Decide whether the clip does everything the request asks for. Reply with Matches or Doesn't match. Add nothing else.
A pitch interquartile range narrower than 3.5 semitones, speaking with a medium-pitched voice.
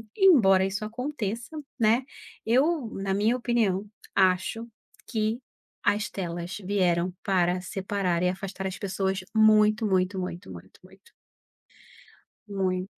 Doesn't match